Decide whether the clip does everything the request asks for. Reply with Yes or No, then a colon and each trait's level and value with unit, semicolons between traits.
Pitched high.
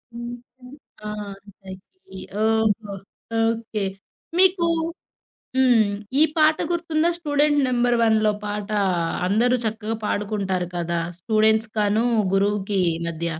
Yes: high, 220 Hz